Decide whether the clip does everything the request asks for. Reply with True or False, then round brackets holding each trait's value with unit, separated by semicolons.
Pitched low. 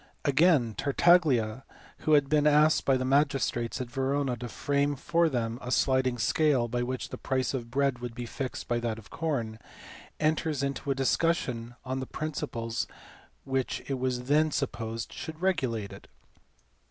True (130 Hz)